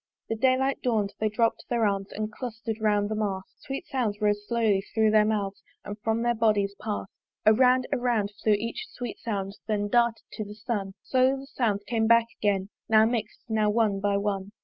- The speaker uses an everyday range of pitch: No, narrow, 2.2 semitones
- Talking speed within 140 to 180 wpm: No, average, 195 wpm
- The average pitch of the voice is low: No, high, 215 Hz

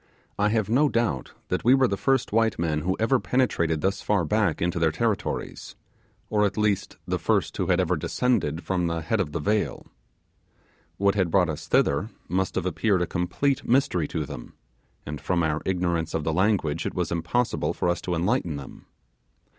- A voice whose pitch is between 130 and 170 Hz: No, very low, 90 Hz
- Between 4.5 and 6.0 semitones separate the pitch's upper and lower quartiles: Yes, average, 4.8 semitones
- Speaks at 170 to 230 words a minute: Yes, average, 195 wpm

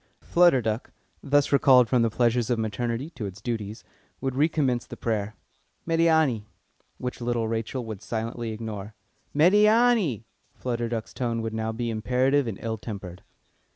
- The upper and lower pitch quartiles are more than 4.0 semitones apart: No, average, 3.2 semitones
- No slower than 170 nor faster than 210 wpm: No, average, 150 wpm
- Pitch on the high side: No, low, 120 Hz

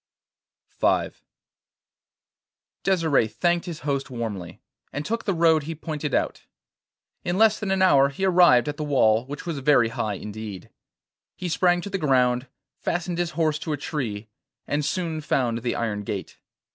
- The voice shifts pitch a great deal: Yes, wide, 6.2 semitones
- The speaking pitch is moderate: Yes, medium, 150 Hz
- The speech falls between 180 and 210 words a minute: No, average, 160 wpm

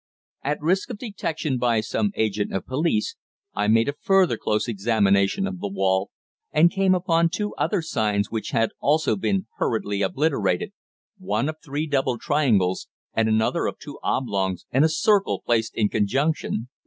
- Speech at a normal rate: Yes, average, 165 wpm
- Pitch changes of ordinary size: No, wide, 7.7 semitones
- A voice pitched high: No, low, 130 Hz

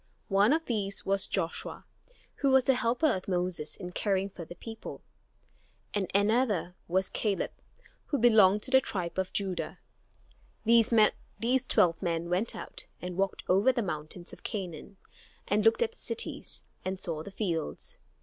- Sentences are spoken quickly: No, average, 160 wpm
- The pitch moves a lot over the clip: No, average, 4.3 semitones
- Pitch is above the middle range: Yes, high, 200 Hz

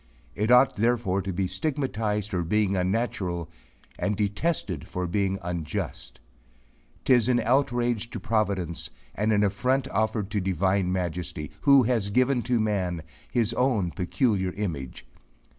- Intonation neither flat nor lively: Yes, average, 4.6 semitones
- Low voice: Yes, low, 105 Hz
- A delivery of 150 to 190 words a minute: No, slow, 135 wpm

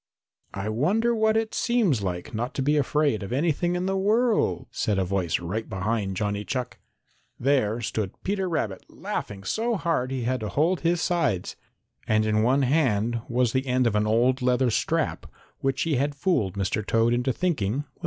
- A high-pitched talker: No, low, 125 Hz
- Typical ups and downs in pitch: No, wide, 7.4 semitones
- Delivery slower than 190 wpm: No, average, 195 wpm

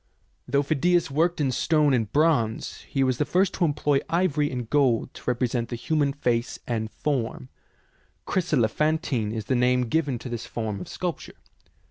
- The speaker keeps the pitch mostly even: No, average, 4.4 semitones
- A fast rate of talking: No, average, 175 wpm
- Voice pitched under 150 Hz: Yes, low, 135 Hz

